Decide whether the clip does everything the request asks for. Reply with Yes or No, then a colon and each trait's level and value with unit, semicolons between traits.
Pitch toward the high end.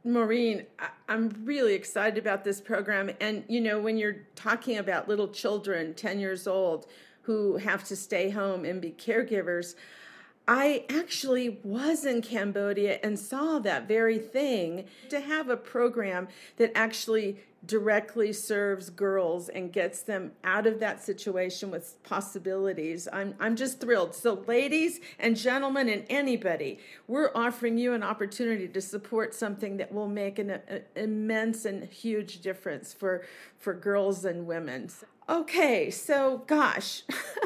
Yes: high, 210 Hz